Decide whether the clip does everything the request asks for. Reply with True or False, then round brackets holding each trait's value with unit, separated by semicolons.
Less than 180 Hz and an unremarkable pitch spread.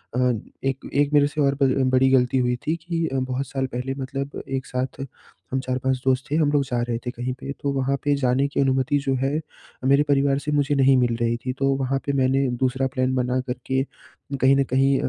False (135 Hz; 1.4 semitones)